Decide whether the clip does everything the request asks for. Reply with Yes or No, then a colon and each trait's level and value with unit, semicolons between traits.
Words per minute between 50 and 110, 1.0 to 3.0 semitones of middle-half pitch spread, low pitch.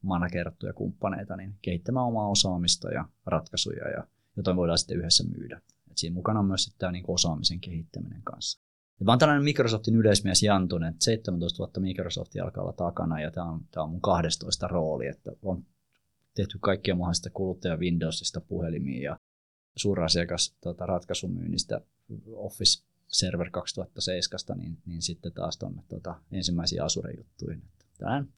No: average, 145 wpm; average, 2.7 semitones; very low, 90 Hz